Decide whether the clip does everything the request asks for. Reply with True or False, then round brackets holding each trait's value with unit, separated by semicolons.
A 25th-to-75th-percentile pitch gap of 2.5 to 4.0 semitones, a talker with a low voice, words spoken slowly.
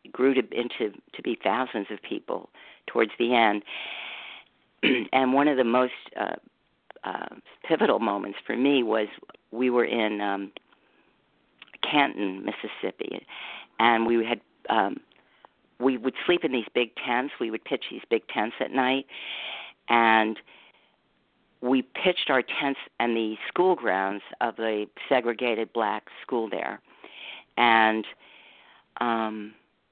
True (3.1 semitones; 120 Hz; 130 wpm)